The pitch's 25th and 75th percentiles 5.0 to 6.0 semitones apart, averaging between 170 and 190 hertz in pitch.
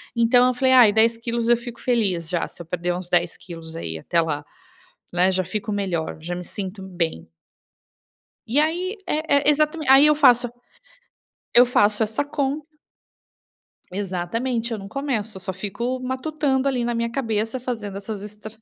No: average, 5.3 semitones; high, 225 Hz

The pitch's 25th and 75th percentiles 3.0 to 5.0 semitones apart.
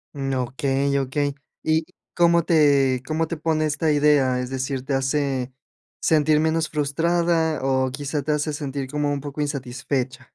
No: narrow, 2.6 semitones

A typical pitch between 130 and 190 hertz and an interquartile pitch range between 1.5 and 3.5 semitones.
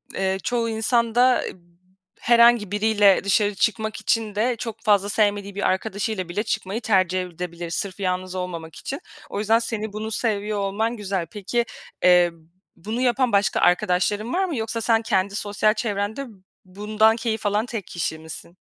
No: high, 210 Hz; average, 2.9 semitones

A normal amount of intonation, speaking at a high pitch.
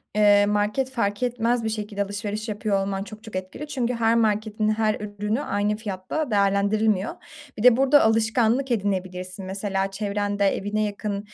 No: narrow, 1.9 semitones; high, 210 Hz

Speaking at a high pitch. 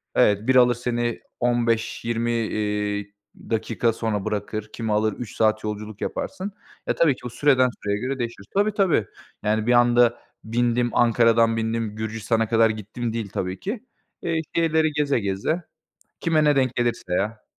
No: low, 115 Hz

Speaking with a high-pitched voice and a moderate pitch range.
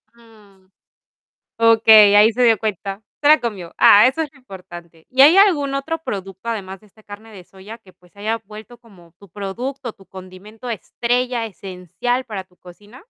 Yes: high, 215 Hz; average, 4.1 semitones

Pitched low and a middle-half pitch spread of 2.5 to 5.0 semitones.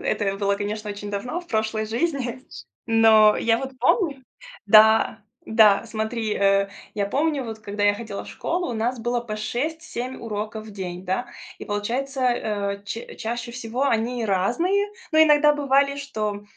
No: high, 225 Hz; average, 3.9 semitones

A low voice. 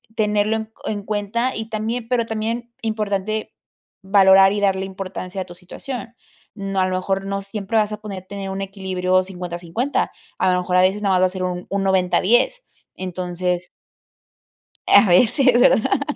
No: high, 195 Hz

